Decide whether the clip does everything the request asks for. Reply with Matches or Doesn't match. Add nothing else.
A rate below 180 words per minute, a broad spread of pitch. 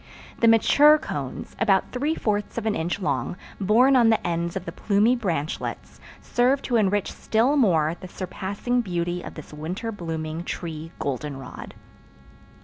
Matches